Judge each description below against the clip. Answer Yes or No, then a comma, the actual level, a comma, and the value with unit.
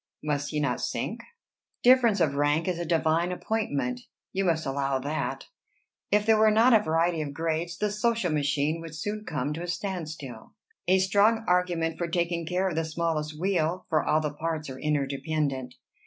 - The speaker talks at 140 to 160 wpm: No, average, 185 wpm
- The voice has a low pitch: No, medium, 165 Hz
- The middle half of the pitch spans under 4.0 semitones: Yes, average, 3.6 semitones